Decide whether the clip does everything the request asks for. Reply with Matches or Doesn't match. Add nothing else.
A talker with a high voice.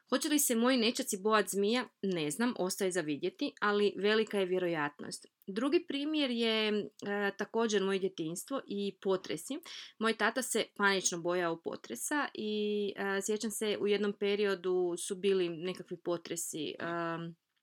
Matches